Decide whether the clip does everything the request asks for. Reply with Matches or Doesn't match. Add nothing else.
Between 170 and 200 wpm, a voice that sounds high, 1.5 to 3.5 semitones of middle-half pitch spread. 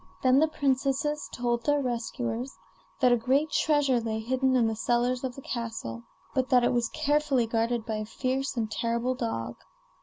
Matches